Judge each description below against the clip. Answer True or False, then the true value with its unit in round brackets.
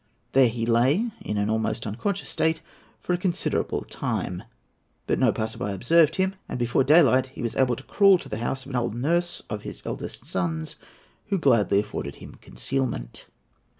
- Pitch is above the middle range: False (130 Hz)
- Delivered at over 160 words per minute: True (185 wpm)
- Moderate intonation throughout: False (6.9 semitones)